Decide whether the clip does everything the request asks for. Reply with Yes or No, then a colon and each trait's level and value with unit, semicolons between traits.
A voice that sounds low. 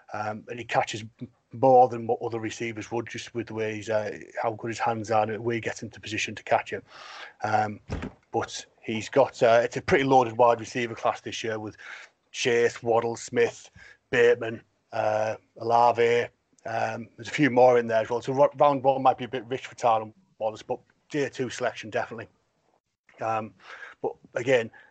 Yes: low, 115 Hz